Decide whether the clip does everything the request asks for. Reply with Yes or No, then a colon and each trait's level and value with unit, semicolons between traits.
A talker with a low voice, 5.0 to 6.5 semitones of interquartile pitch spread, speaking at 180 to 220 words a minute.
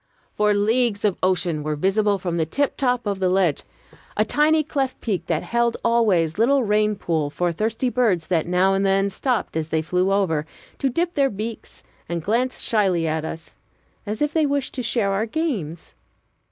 No: high, 205 Hz; wide, 5.4 semitones; average, 185 wpm